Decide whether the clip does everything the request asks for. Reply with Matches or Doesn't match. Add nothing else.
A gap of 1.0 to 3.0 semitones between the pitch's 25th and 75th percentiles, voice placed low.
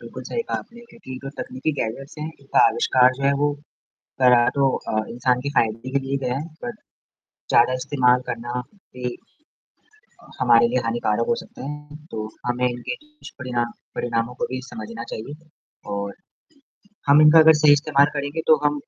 Doesn't match